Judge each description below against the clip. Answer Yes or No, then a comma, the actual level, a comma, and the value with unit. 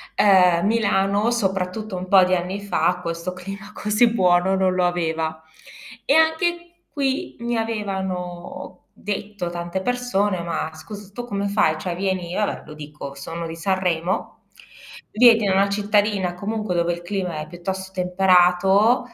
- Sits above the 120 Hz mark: Yes, high, 190 Hz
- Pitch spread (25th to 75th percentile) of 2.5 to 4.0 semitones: Yes, average, 2.9 semitones